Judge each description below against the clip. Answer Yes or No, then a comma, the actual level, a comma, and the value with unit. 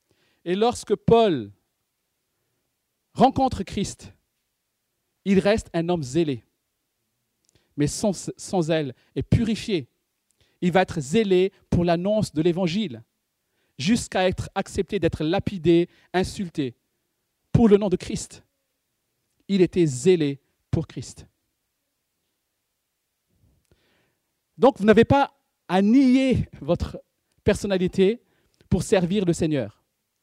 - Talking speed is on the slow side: Yes, slow, 105 wpm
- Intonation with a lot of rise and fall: Yes, wide, 6.5 semitones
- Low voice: No, medium, 175 Hz